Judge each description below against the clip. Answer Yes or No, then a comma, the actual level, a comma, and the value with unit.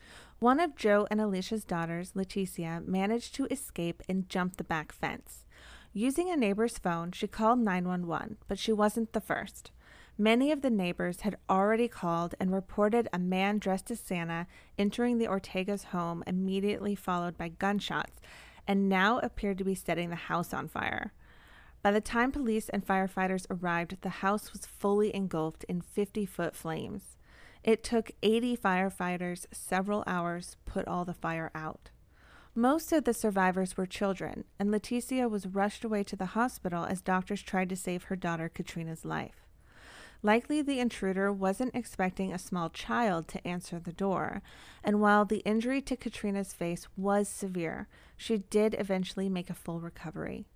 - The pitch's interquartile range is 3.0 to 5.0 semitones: Yes, average, 3.3 semitones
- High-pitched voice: Yes, high, 195 Hz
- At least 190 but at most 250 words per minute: No, average, 165 wpm